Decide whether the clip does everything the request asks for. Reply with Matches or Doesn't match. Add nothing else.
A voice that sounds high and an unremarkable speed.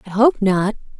Matches